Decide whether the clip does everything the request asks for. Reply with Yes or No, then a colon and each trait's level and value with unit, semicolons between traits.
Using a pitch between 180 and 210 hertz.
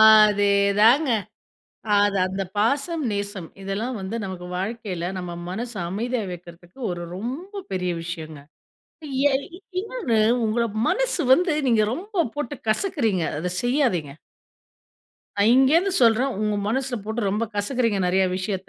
No: high, 220 Hz